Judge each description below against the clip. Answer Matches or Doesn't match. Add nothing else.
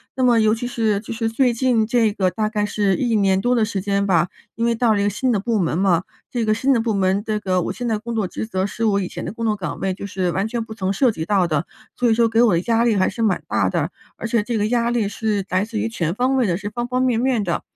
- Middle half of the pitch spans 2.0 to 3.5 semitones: Matches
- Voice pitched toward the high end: Matches